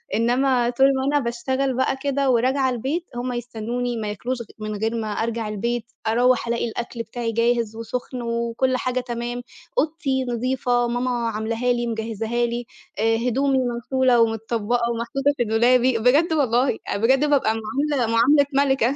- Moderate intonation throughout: No, narrow, 2.2 semitones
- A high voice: Yes, high, 240 Hz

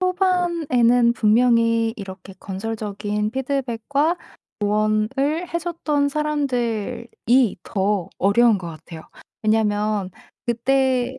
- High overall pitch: Yes, high, 235 Hz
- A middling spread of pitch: Yes, average, 4.7 semitones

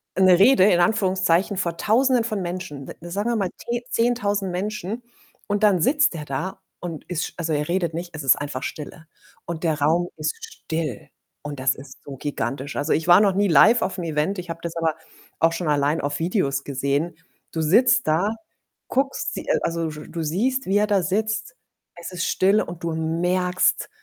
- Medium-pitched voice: Yes, medium, 175 Hz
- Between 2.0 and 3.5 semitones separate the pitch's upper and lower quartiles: No, average, 4.5 semitones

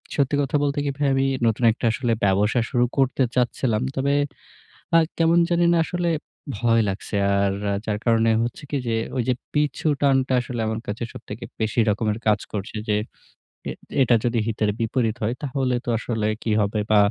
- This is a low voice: Yes, low, 120 Hz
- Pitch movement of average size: Yes, average, 3.7 semitones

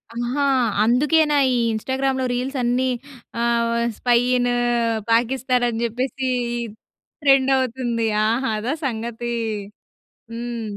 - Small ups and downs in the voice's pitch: Yes, narrow, 2.0 semitones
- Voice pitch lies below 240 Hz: No, high, 245 Hz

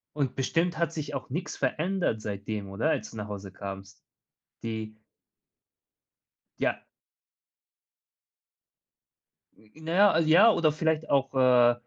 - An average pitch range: No, wide, 6.9 semitones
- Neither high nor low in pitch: No, low, 130 Hz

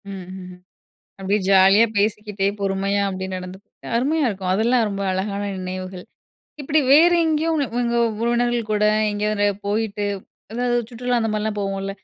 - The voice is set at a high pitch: Yes, high, 210 Hz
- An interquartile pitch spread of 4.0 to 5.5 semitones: No, average, 3.5 semitones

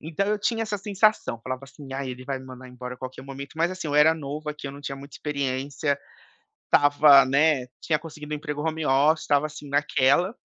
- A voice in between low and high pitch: Yes, medium, 145 Hz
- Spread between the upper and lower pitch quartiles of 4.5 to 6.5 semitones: No, narrow, 2.6 semitones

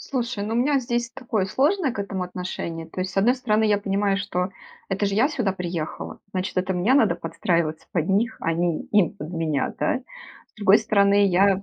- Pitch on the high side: Yes, high, 195 Hz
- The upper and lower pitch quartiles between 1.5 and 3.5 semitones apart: No, average, 4.0 semitones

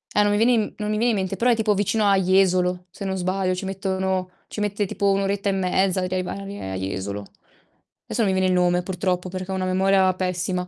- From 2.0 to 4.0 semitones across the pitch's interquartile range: No, narrow, 1.5 semitones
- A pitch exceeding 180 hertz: Yes, high, 190 Hz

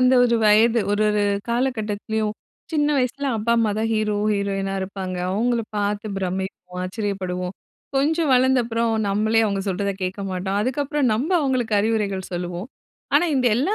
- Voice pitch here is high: Yes, high, 215 Hz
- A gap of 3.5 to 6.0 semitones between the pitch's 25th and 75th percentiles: Yes, average, 4.0 semitones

